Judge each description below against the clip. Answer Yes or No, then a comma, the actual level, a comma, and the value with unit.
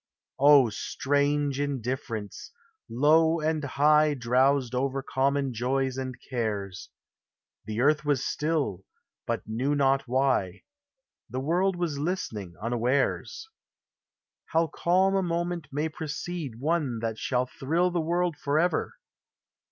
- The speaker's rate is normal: No, slow, 130 wpm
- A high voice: No, medium, 140 Hz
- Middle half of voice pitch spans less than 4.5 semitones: Yes, average, 4.0 semitones